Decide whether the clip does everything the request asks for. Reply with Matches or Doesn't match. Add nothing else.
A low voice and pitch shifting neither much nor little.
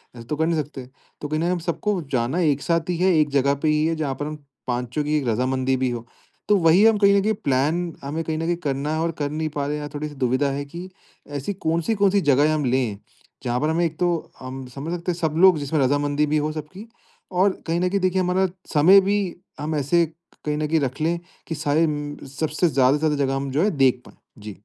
Doesn't match